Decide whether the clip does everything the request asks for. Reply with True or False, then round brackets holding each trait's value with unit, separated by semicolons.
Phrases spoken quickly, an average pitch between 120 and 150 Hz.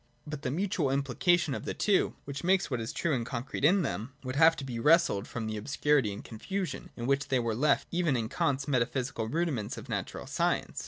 True (225 wpm; 140 Hz)